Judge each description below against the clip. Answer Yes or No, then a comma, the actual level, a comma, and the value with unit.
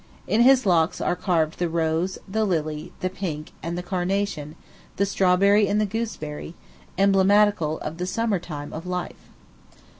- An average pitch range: Yes, average, 3.7 semitones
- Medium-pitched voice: Yes, medium, 180 Hz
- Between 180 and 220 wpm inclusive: No, average, 155 wpm